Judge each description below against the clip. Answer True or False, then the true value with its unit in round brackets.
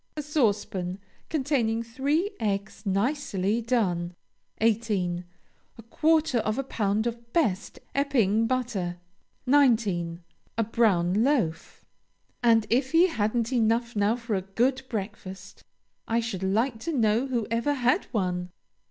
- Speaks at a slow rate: True (125 wpm)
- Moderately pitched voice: False (225 Hz)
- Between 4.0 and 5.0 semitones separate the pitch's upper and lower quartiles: True (4.3 semitones)